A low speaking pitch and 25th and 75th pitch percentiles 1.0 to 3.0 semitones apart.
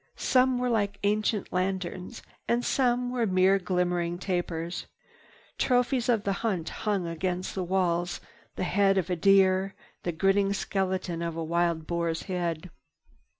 No: medium, 185 Hz; average, 2.7 semitones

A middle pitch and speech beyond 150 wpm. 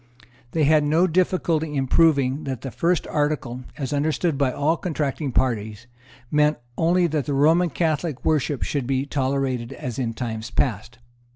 Yes: medium, 145 Hz; average, 165 wpm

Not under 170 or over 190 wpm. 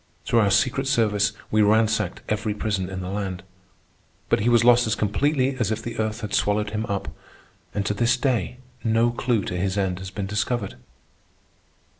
Yes: average, 185 wpm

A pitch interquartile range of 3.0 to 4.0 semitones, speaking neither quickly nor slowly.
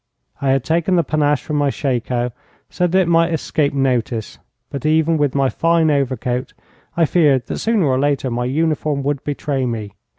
Yes: average, 3.6 semitones; average, 185 wpm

